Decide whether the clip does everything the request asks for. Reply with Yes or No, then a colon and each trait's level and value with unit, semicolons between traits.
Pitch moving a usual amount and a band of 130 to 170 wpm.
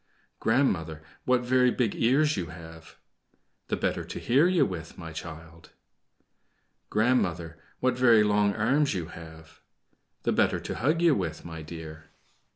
No: wide, 7.6 semitones; average, 145 wpm